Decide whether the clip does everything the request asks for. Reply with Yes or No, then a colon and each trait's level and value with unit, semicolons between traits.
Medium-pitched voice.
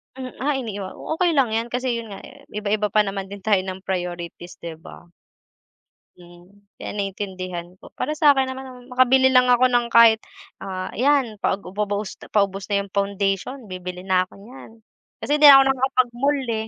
No: high, 210 Hz